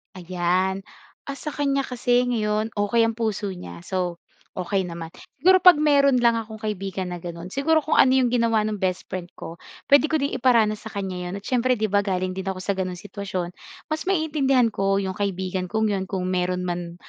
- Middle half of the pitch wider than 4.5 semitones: Yes, average, 5.1 semitones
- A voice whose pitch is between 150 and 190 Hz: No, high, 205 Hz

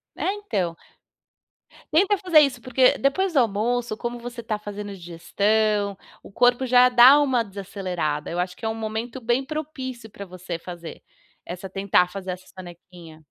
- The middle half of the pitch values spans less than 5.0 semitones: No, average, 5.3 semitones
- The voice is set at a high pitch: Yes, high, 215 Hz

